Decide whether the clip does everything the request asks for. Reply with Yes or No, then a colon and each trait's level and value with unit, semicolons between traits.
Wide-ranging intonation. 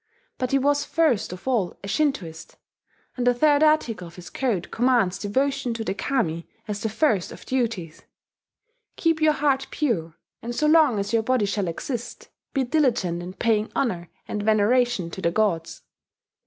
Yes: wide, 6.0 semitones